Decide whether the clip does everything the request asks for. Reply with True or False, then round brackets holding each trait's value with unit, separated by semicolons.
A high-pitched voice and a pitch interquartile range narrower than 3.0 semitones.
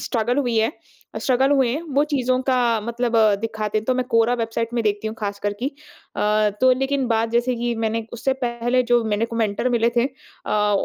True (235 Hz; 2.6 semitones)